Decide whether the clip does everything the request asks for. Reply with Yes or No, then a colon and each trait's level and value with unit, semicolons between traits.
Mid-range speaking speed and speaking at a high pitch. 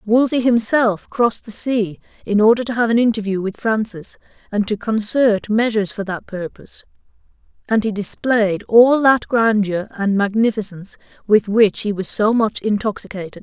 Yes: average, 155 wpm; high, 215 Hz